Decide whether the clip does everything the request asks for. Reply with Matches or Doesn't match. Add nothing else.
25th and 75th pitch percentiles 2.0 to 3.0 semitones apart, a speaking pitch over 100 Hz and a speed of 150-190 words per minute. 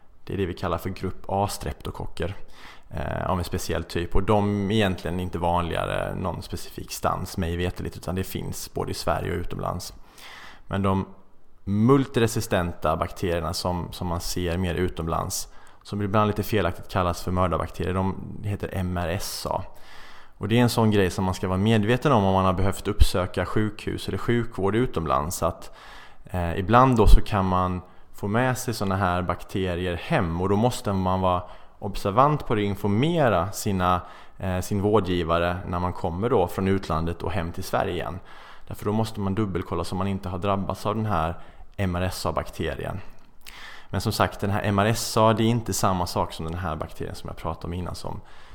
Doesn't match